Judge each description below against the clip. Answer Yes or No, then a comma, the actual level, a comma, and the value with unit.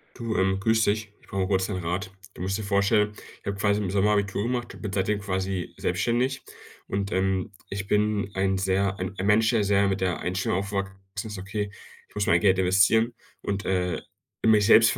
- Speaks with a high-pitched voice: No, low, 100 Hz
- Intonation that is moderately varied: No, narrow, 1.7 semitones